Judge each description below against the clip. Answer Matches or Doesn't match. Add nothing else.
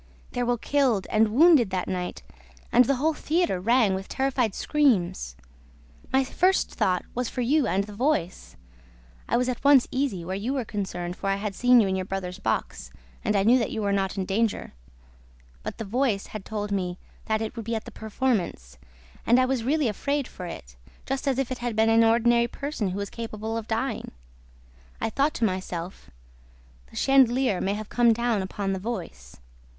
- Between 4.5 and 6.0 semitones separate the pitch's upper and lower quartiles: Matches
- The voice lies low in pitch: Doesn't match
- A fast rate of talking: Doesn't match